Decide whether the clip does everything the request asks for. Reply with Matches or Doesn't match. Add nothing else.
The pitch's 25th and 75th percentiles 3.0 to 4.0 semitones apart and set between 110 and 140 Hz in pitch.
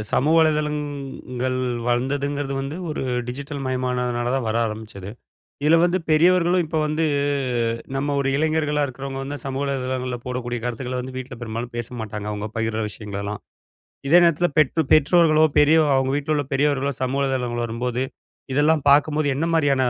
Matches